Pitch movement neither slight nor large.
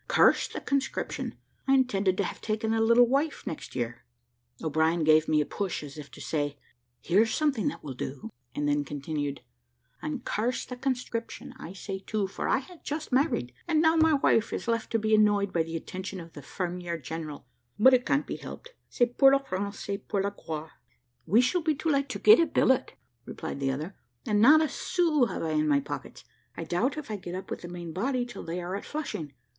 No: wide, 8.3 semitones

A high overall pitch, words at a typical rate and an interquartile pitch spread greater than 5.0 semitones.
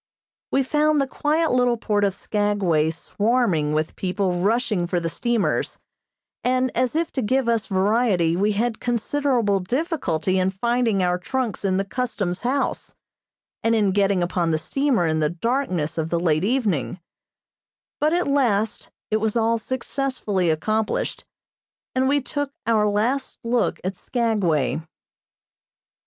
Yes: high, 215 Hz; average, 145 wpm; wide, 5.6 semitones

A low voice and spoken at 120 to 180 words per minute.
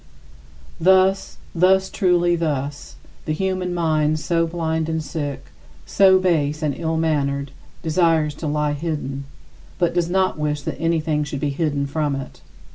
No: medium, 160 Hz; average, 145 wpm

